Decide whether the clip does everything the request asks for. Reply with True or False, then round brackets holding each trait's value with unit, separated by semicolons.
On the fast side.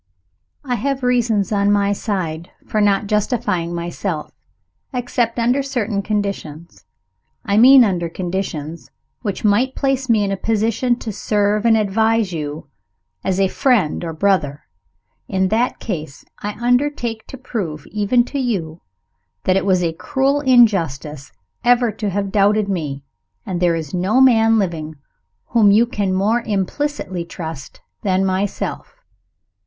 False (145 wpm)